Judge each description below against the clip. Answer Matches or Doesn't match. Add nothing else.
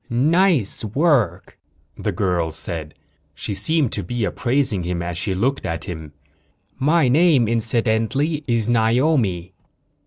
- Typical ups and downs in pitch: Doesn't match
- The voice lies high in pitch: Doesn't match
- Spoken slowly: Matches